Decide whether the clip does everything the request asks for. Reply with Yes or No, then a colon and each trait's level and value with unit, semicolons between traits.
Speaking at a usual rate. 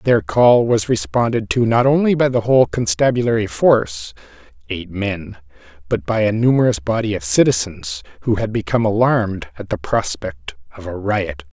Yes: average, 160 wpm